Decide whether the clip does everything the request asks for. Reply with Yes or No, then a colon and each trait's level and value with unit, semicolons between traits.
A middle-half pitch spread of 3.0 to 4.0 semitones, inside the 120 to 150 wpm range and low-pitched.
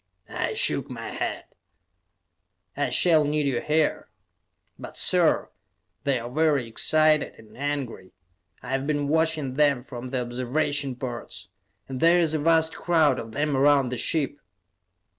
No: average, 3.4 semitones; average, 145 wpm; medium, 145 Hz